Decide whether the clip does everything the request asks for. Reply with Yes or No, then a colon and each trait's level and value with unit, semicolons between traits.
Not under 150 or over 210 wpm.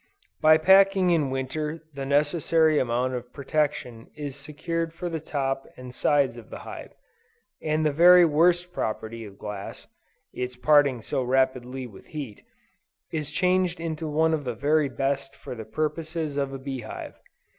Yes: average, 160 wpm